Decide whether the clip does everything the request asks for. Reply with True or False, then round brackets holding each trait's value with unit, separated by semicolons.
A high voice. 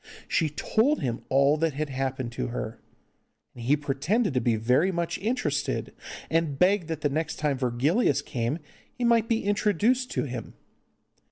False (150 Hz)